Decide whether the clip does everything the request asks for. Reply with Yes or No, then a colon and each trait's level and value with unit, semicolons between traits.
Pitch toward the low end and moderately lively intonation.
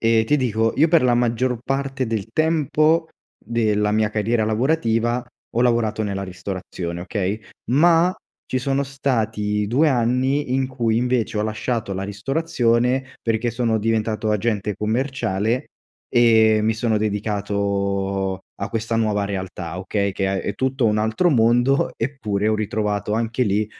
Yes: low, 115 Hz; average, 3.4 semitones